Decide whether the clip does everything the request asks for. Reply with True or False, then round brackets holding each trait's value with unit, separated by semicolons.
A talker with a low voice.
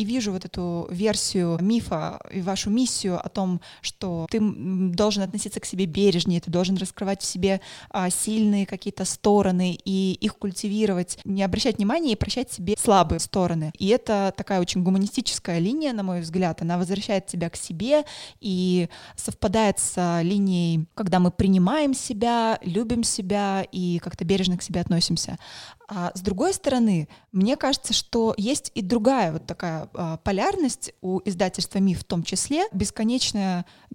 False (195 Hz)